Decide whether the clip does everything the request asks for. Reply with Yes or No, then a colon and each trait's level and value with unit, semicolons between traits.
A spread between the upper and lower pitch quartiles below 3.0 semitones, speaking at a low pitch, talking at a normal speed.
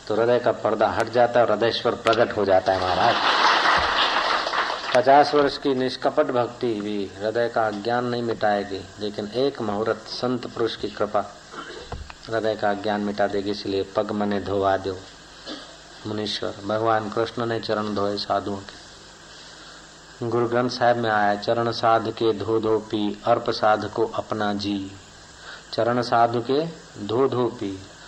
Yes: narrow, 2.6 semitones; low, 110 Hz; average, 150 wpm